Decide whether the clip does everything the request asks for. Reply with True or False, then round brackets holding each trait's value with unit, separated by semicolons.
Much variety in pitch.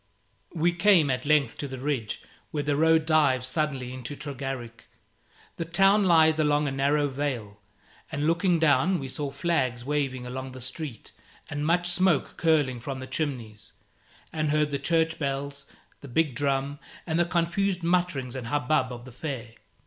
False (3.8 semitones)